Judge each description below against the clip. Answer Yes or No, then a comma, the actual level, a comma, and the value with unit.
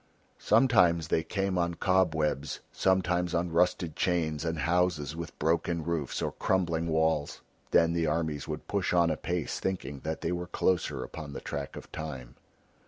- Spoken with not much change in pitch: Yes, narrow, 2.3 semitones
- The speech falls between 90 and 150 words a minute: No, average, 160 wpm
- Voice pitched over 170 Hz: No, very low, 85 Hz